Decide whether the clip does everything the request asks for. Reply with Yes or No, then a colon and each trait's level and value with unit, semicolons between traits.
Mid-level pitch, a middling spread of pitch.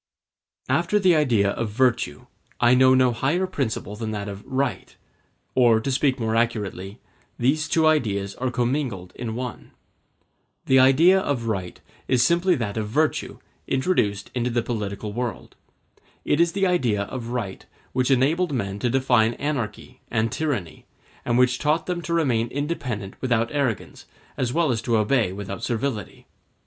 No: low, 125 Hz; average, 4.3 semitones